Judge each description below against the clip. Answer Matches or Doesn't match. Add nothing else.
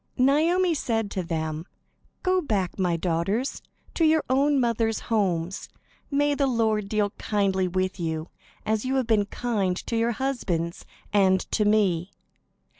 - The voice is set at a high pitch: Matches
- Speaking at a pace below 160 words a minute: Matches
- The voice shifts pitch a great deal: Matches